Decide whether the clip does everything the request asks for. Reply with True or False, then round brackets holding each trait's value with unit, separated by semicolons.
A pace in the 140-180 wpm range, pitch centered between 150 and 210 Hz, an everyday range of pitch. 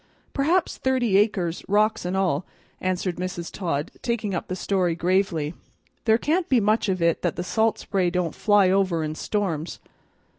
True (170 wpm; 190 Hz; 3.6 semitones)